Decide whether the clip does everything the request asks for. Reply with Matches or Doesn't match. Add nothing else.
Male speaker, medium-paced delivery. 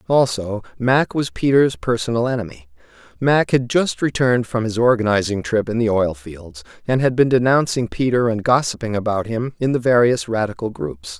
Matches